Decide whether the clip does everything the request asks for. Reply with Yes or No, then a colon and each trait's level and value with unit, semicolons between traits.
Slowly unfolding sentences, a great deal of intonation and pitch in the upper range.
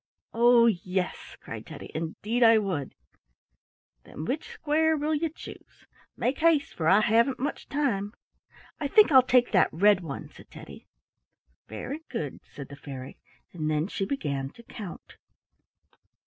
No: average, 145 wpm; wide, 9.0 semitones; high, 215 Hz